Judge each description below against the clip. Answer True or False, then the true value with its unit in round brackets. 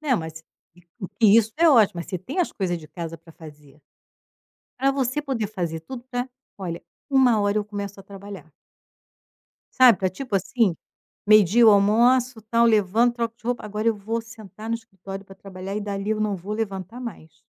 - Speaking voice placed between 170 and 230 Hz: True (210 Hz)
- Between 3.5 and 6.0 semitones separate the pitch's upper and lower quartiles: True (3.8 semitones)